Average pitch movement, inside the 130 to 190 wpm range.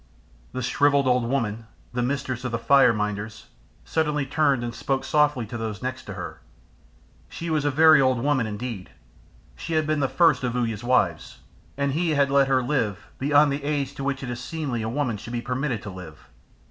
No: average, 3.7 semitones; average, 200 wpm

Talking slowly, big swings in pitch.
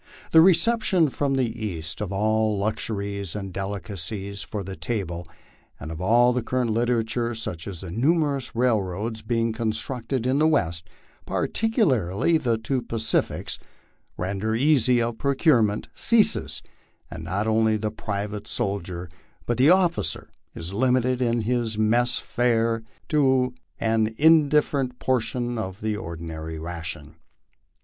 No: slow, 130 wpm; average, 4.2 semitones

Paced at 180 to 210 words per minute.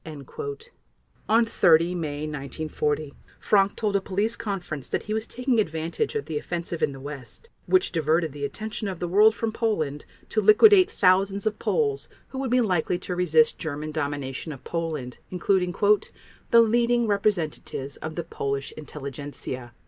No: average, 155 wpm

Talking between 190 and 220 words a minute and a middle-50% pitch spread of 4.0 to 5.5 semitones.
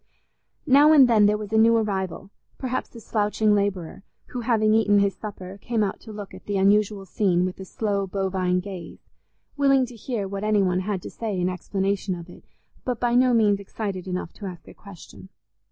No: average, 200 wpm; narrow, 2.6 semitones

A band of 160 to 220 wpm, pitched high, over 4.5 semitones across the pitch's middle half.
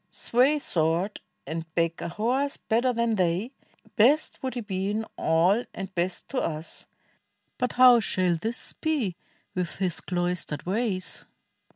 No: average, 145 wpm; high, 195 Hz; wide, 5.6 semitones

